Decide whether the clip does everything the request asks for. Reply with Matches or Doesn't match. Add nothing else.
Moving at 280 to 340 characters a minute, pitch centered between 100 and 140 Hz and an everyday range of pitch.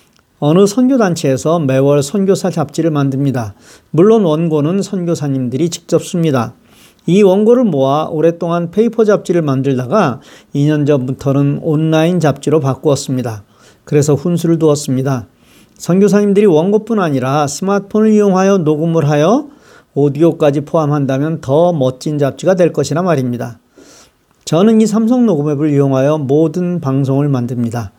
Doesn't match